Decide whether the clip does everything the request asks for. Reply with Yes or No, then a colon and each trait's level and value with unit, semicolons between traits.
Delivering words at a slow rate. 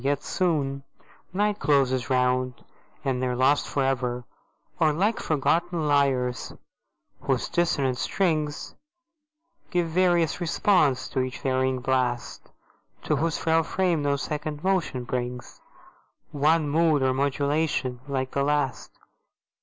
Yes: slow, 120 wpm